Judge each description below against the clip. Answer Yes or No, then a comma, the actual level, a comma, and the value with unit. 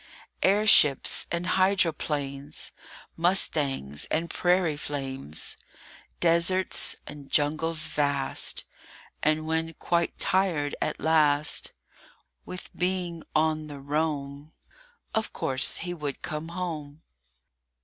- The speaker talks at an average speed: No, slow, 95 wpm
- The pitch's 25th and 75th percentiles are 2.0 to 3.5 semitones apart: Yes, average, 3.0 semitones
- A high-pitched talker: No, medium, 155 Hz